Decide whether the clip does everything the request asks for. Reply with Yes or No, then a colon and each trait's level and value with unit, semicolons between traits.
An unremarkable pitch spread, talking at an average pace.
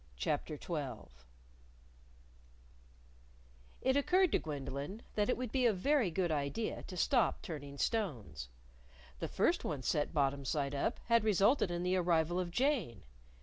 No: wide, 8.2 semitones; average, 145 wpm